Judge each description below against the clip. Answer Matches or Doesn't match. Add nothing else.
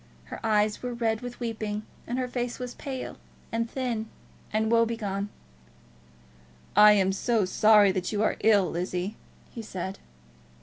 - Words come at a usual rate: Matches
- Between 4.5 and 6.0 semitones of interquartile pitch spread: Doesn't match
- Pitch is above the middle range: Matches